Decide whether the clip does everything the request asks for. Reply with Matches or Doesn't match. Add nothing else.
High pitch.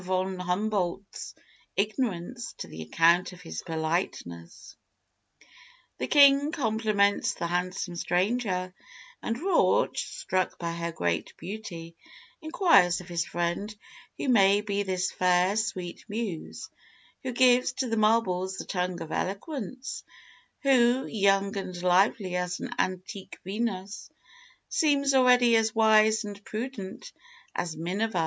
Matches